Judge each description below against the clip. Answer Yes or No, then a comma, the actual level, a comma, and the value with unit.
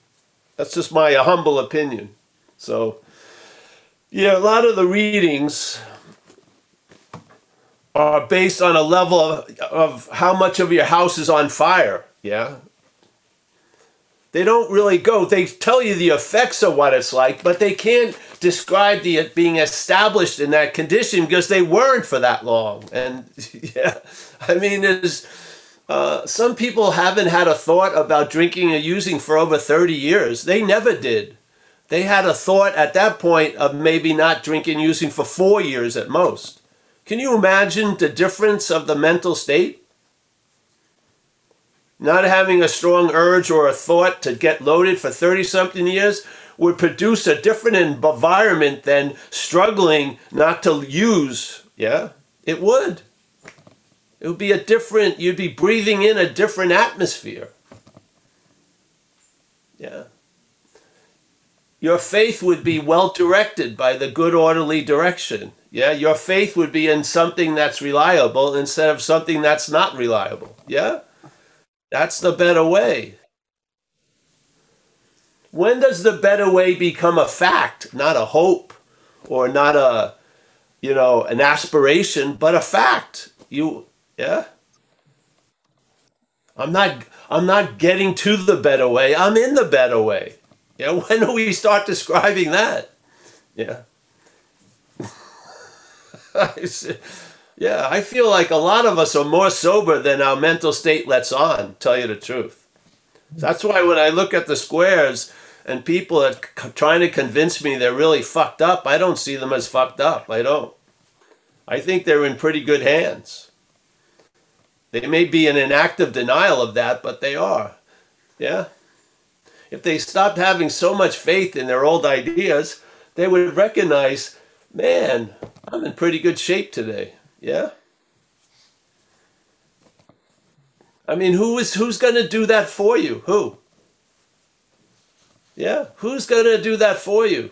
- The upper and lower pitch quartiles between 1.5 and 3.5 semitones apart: No, average, 4.7 semitones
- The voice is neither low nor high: Yes, medium, 175 Hz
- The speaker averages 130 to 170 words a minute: Yes, average, 145 wpm